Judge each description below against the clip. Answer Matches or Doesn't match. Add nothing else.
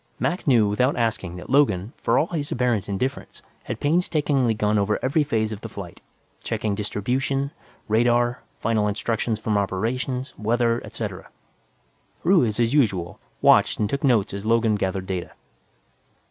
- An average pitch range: Matches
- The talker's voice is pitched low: Matches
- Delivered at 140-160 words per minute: Matches